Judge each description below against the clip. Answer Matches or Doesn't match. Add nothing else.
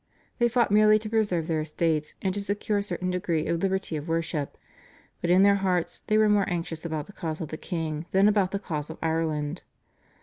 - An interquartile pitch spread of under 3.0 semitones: Doesn't match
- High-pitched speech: Doesn't match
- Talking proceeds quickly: Matches